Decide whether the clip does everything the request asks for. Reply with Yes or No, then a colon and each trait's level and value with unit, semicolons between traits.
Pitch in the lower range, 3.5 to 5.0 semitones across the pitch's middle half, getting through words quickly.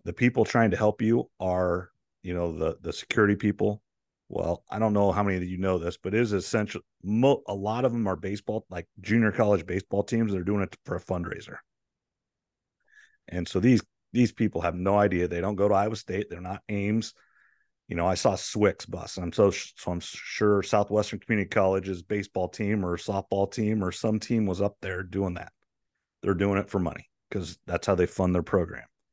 No: low, 100 Hz; average, 2.8 semitones; fast, 210 wpm